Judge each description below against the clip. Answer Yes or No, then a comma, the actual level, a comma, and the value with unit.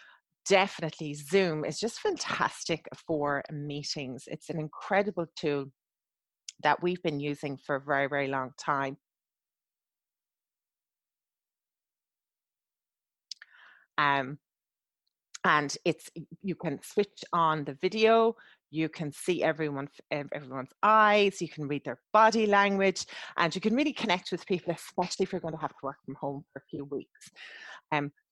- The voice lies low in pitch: No, medium, 155 Hz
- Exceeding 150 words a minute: No, slow, 135 wpm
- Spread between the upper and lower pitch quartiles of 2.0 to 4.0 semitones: No, average, 4.4 semitones